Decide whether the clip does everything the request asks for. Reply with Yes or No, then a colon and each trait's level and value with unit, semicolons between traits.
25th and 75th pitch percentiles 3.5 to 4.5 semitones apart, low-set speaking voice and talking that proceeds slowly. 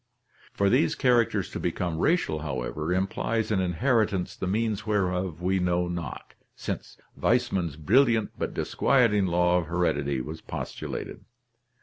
Yes: average, 4.0 semitones; very low, 90 Hz; slow, 130 wpm